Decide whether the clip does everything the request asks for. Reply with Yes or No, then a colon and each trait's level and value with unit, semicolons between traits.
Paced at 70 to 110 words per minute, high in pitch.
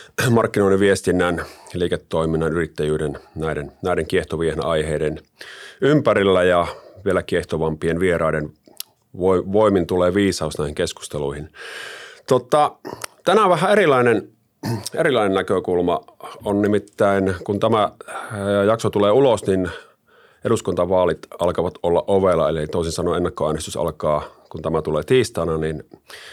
No: average, 105 wpm; very low, 90 Hz